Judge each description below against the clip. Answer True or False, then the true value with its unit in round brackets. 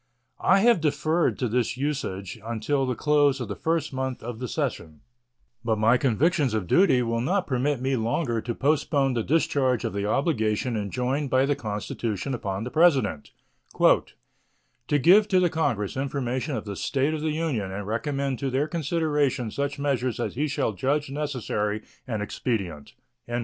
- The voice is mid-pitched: False (130 Hz)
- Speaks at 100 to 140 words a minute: False (170 wpm)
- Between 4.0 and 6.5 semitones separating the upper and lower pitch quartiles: True (4.7 semitones)